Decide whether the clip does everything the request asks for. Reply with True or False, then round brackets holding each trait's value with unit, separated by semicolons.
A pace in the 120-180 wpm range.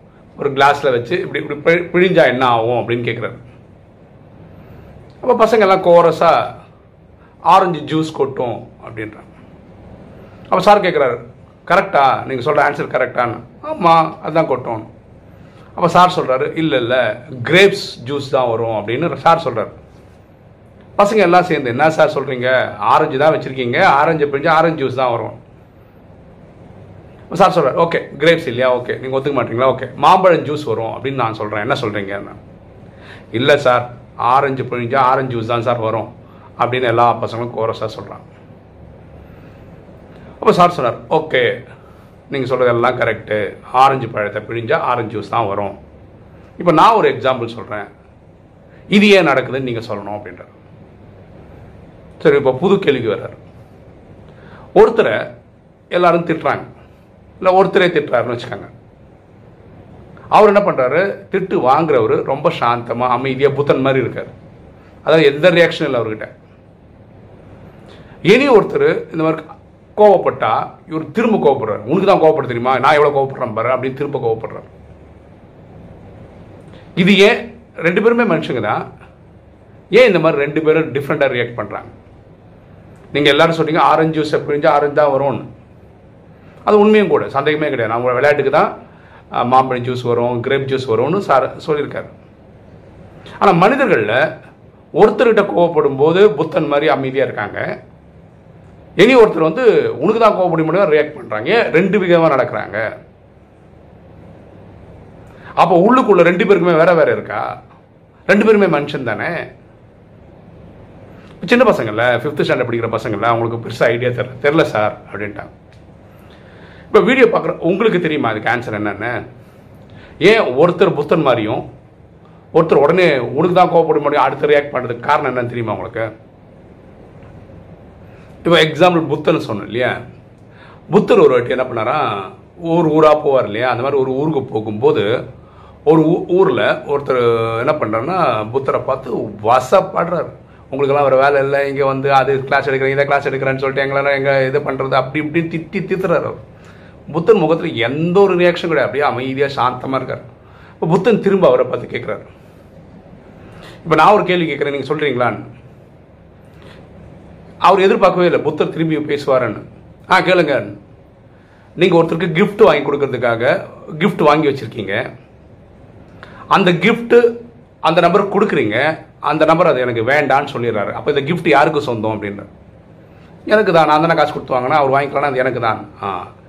True (130 wpm)